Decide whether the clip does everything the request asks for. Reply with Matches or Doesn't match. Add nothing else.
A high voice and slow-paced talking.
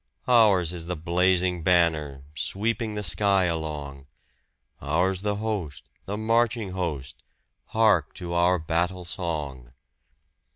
Doesn't match